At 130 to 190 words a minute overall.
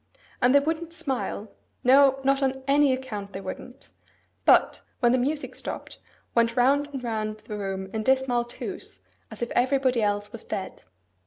Yes: average, 160 wpm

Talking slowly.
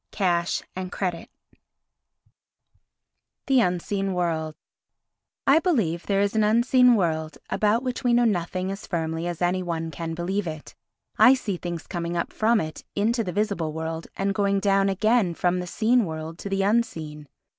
No: average, 165 wpm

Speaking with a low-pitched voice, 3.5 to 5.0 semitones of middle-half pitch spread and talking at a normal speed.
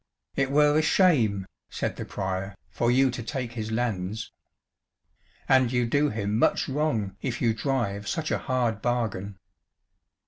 Yes: low, 120 Hz; average, 4.4 semitones; average, 150 wpm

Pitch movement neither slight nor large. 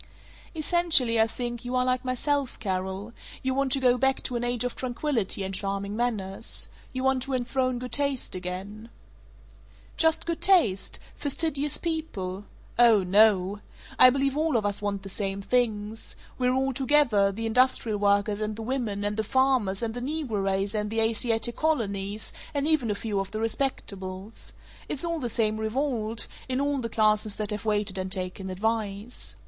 Yes: average, 4.3 semitones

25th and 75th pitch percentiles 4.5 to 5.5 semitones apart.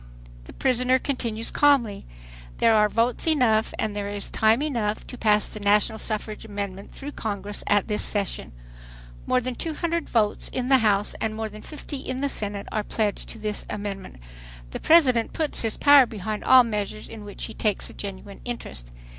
No: average, 3.5 semitones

